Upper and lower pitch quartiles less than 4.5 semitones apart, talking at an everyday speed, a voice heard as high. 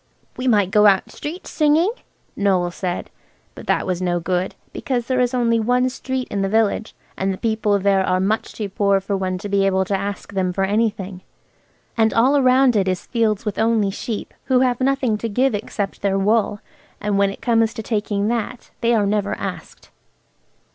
Yes: average, 3.3 semitones; average, 195 wpm; high, 210 Hz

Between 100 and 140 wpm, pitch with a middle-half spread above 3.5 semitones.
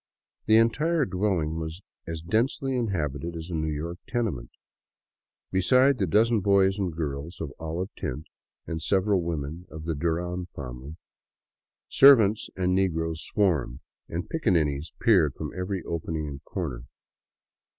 Yes: slow, 135 wpm; average, 4.2 semitones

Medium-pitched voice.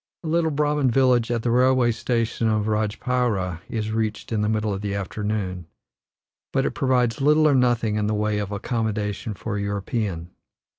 No: low, 110 Hz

